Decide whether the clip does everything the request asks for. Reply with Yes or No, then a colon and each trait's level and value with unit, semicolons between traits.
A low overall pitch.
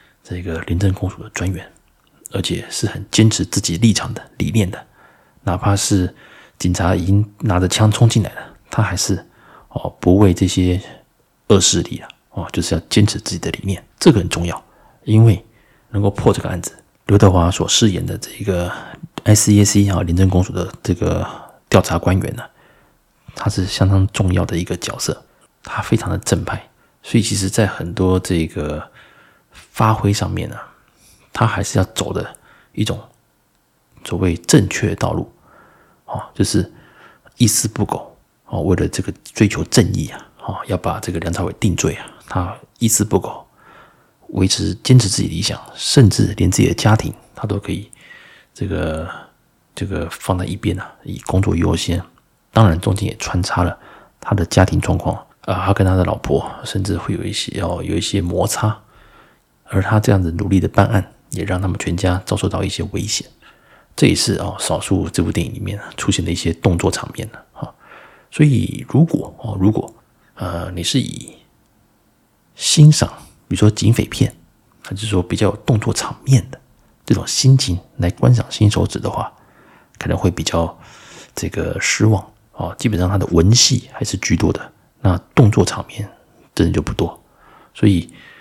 Yes: low, 100 Hz